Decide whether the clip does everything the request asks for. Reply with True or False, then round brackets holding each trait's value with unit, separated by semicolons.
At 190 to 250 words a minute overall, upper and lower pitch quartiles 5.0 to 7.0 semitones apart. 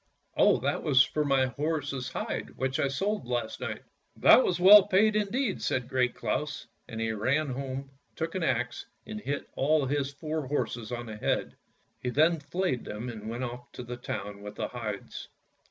False (200 wpm; 4.4 semitones)